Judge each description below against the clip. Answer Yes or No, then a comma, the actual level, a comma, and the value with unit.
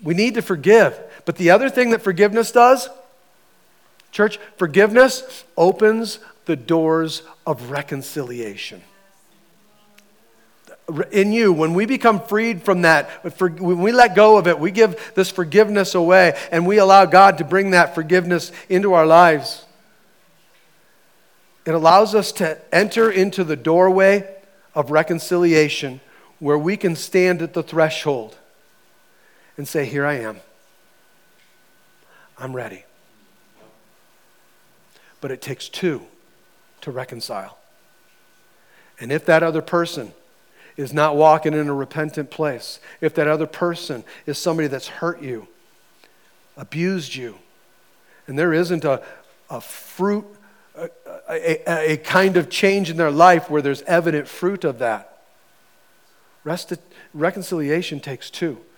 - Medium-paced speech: No, slow, 130 wpm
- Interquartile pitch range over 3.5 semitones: Yes, average, 4.0 semitones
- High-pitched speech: No, medium, 175 Hz